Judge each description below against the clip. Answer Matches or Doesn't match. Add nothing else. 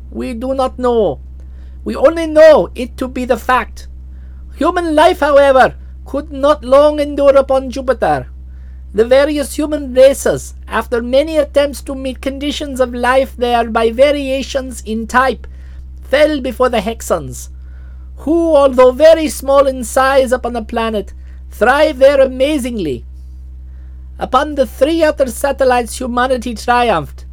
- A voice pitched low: Doesn't match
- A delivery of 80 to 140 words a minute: Matches